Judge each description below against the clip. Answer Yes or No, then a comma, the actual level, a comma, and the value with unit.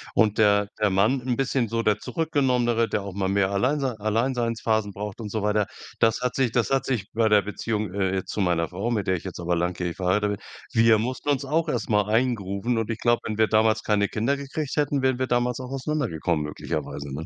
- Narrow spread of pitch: No, average, 3.7 semitones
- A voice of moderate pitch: No, low, 110 Hz